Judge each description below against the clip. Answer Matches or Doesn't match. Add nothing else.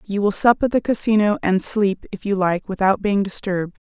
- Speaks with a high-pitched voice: Matches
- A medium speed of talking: Doesn't match